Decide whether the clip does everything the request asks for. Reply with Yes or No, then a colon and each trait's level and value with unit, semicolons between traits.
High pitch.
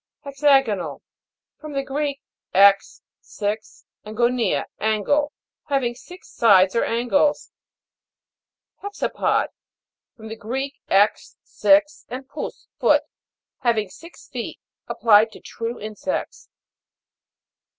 Yes: high, 240 Hz